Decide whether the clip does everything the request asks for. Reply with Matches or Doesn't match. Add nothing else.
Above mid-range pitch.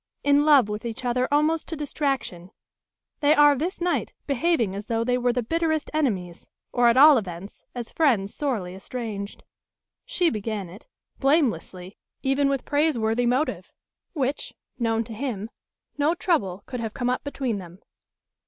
Matches